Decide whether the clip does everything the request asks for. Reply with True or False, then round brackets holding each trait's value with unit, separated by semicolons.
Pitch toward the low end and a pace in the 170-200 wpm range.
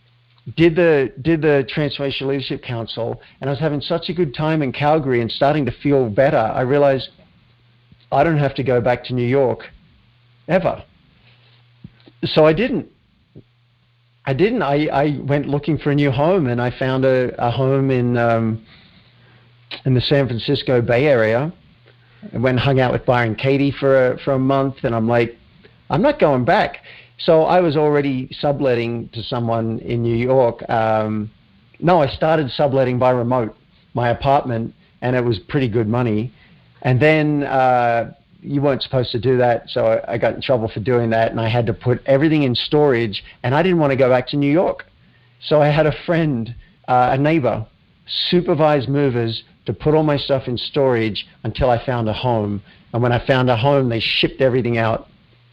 True (130 Hz; 185 wpm)